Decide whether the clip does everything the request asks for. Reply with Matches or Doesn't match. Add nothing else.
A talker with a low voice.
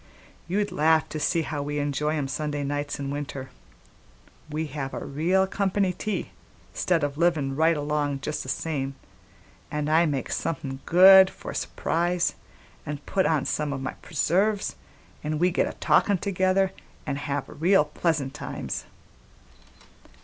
Doesn't match